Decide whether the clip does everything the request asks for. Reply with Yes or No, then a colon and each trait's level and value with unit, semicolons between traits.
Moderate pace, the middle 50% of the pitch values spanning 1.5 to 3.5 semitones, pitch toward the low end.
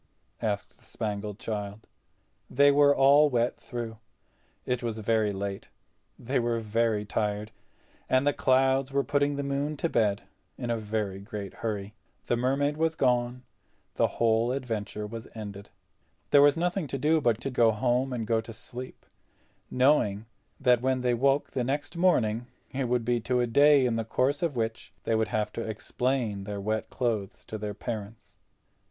No: average, 170 wpm; average, 3.9 semitones; low, 120 Hz